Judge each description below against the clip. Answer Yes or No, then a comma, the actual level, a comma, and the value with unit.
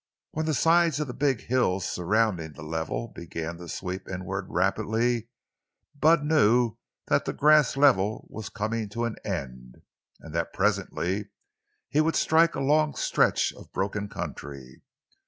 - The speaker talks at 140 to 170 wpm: Yes, average, 150 wpm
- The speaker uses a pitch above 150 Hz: No, low, 105 Hz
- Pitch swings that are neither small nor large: No, wide, 7.3 semitones